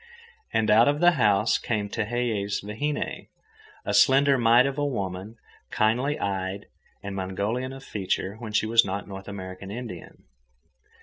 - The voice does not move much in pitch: No, average, 4.0 semitones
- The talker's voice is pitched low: Yes, low, 110 Hz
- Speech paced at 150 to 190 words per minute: No, average, 140 wpm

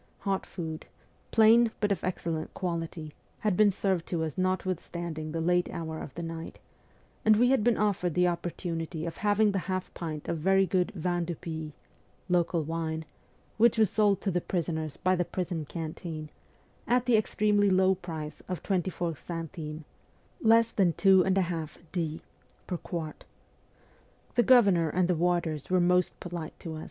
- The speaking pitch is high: No, medium, 175 Hz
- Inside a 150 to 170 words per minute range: Yes, average, 160 wpm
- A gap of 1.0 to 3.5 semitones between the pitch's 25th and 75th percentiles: Yes, average, 2.9 semitones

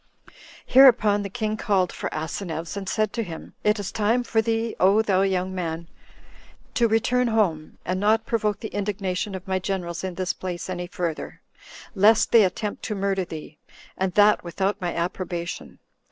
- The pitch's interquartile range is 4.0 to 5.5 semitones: No, average, 3.1 semitones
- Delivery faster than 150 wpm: Yes, average, 170 wpm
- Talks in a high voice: Yes, high, 195 Hz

